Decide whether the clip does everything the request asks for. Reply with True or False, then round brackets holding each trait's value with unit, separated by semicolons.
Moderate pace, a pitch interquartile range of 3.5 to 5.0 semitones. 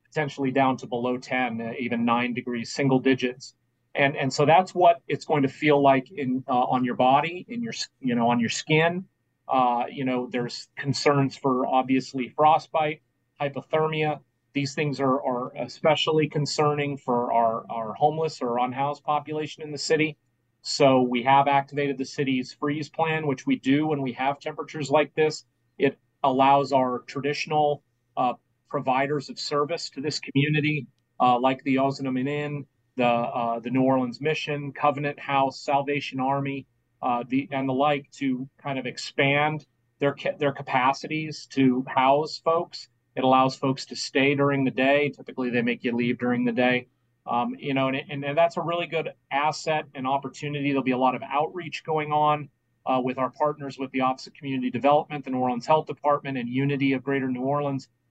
False (180 wpm; 2.7 semitones)